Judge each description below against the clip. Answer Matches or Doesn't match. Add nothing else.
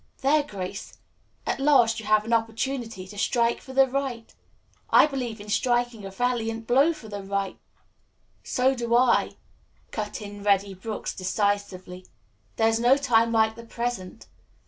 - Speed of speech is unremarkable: Matches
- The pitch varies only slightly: Doesn't match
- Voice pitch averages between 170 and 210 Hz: Doesn't match